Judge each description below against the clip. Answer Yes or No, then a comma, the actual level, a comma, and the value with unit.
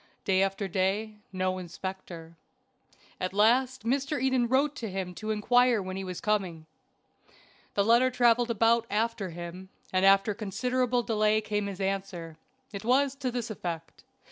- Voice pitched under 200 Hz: No, high, 210 Hz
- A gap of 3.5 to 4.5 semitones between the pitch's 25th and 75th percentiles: Yes, average, 4.2 semitones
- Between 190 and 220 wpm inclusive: No, average, 155 wpm